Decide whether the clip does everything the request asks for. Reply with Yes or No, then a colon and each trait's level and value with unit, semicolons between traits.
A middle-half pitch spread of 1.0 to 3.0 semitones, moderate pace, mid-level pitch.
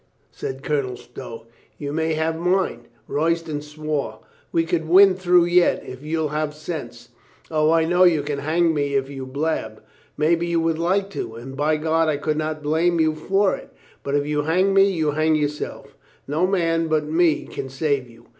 Yes: narrow, 2.5 semitones; average, 190 wpm; medium, 155 Hz